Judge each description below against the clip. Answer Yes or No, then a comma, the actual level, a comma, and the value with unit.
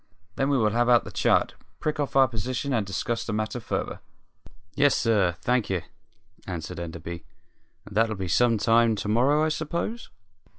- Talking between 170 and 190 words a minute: Yes, average, 175 wpm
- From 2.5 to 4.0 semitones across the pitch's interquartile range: No, average, 4.7 semitones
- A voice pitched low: Yes, low, 115 Hz